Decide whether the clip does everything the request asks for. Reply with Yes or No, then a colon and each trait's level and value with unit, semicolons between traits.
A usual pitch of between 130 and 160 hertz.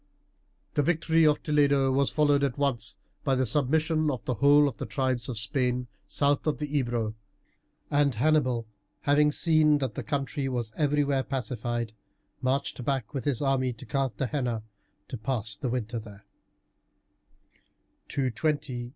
Yes: low, 135 Hz